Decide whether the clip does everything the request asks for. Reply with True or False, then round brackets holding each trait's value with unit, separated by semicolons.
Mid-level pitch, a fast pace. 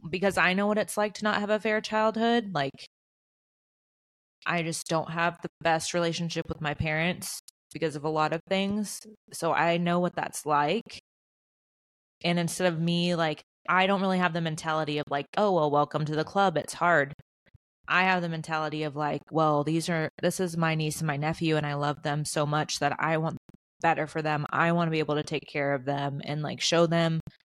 True (165 Hz; 215 wpm)